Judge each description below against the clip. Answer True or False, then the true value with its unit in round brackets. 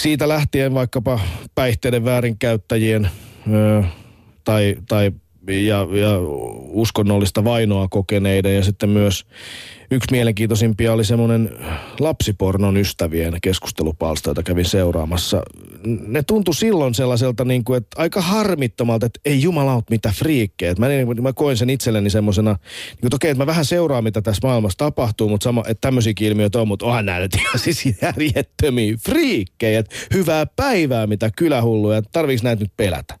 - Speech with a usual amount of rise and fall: True (3.9 semitones)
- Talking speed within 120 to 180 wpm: True (140 wpm)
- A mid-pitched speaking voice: False (115 Hz)